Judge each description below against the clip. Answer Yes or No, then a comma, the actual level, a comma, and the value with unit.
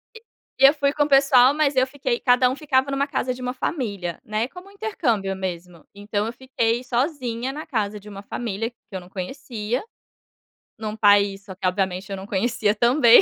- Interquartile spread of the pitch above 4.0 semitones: Yes, average, 4.8 semitones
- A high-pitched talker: Yes, high, 235 Hz